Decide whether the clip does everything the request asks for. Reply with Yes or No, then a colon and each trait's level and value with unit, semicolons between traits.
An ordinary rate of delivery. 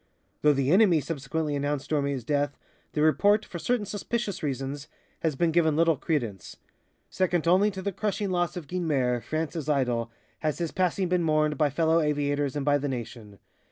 Yes: average, 175 wpm